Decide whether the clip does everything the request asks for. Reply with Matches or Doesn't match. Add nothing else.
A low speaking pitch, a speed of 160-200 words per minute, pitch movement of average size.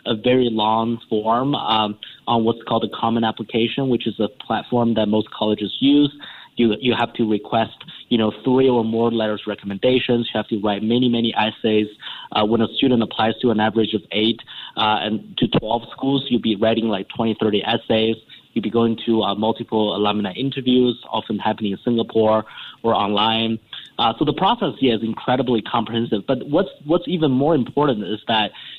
Doesn't match